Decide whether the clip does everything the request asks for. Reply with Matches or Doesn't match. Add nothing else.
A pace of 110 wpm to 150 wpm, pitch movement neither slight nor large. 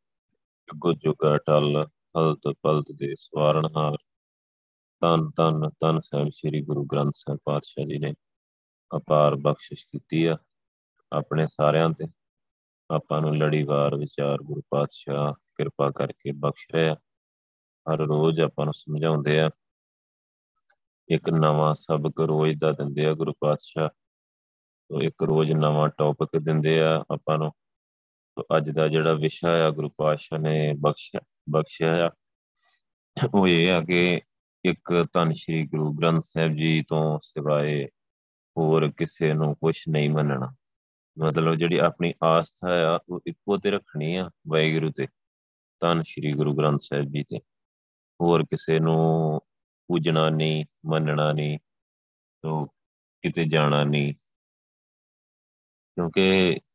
Doesn't match